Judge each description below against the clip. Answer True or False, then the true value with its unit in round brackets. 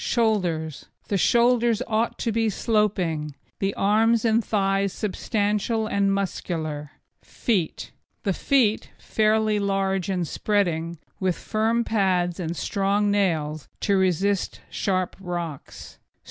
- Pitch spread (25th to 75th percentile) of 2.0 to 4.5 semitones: True (3.5 semitones)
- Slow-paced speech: True (115 wpm)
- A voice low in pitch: False (200 Hz)